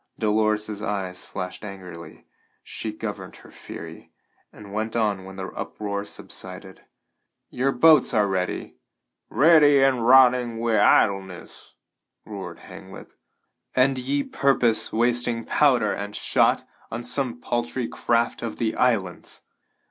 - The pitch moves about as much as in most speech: Yes, average, 3.8 semitones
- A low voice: Yes, low, 115 Hz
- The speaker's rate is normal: No, slow, 120 wpm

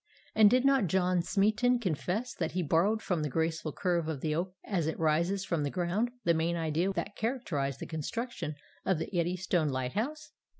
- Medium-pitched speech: Yes, medium, 175 Hz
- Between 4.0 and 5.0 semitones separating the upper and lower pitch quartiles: Yes, average, 4.4 semitones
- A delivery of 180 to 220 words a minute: Yes, average, 185 wpm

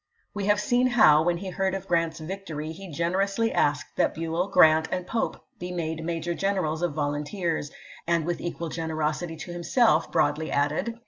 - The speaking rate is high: No, average, 180 wpm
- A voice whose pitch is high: No, medium, 170 Hz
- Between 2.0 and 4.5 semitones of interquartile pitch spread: Yes, average, 3.5 semitones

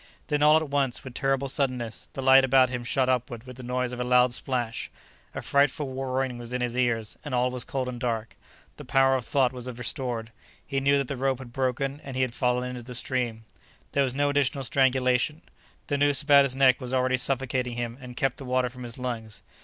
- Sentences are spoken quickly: Yes, fast, 225 wpm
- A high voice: No, low, 130 Hz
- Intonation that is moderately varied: No, narrow, 1.6 semitones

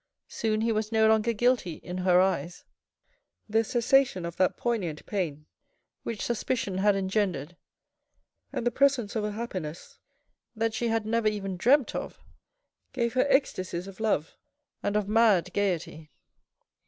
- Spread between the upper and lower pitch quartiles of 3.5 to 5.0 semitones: Yes, average, 3.9 semitones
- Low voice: No, high, 210 Hz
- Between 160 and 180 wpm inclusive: No, average, 145 wpm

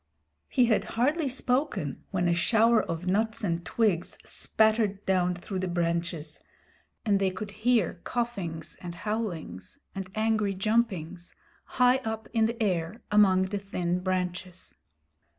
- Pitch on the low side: No, high, 195 Hz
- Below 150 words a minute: Yes, slow, 135 wpm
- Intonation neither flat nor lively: Yes, average, 4.1 semitones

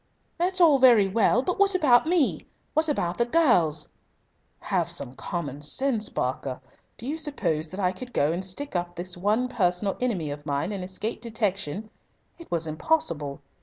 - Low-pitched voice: No, high, 200 Hz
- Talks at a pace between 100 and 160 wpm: No, average, 170 wpm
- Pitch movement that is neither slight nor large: No, wide, 7.4 semitones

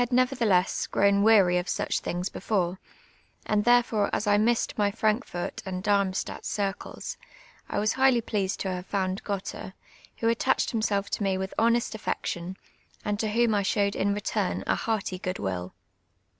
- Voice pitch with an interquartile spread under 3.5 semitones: Yes, average, 2.7 semitones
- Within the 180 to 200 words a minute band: No, average, 165 wpm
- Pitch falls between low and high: No, high, 205 Hz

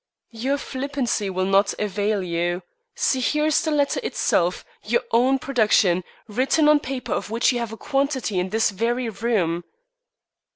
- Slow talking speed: No, average, 160 wpm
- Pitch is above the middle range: Yes, high, 230 Hz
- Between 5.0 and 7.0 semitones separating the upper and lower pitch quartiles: Yes, wide, 5.4 semitones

